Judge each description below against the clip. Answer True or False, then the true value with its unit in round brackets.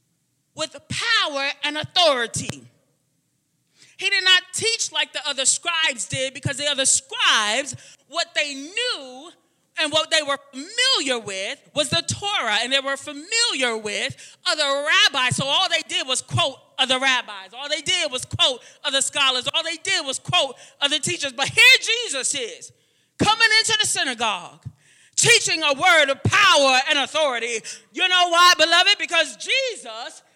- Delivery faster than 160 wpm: False (155 wpm)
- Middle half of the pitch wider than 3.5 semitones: True (5.1 semitones)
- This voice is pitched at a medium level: False (300 Hz)